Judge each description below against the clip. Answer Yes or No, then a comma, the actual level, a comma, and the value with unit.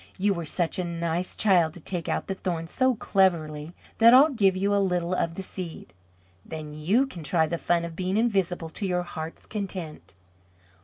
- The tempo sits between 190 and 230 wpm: Yes, average, 195 wpm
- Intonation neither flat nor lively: Yes, average, 3.0 semitones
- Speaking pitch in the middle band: Yes, medium, 180 Hz